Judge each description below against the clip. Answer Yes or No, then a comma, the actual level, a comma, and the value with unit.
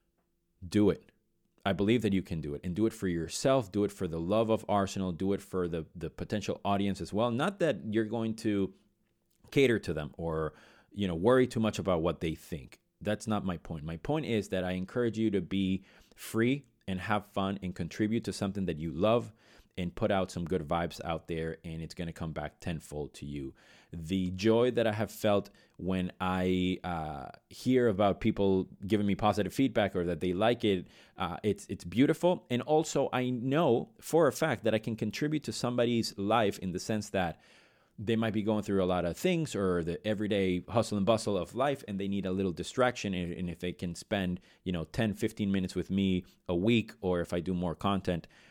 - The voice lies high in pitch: No, low, 100 Hz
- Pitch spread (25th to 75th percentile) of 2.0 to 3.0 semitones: No, average, 3.8 semitones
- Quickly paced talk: Yes, fast, 215 wpm